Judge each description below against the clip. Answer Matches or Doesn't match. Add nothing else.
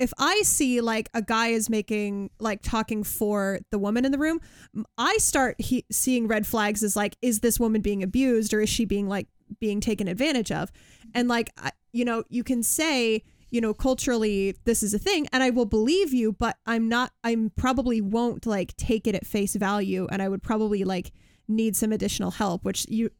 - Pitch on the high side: Matches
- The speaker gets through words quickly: Matches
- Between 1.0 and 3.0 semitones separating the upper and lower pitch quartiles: Matches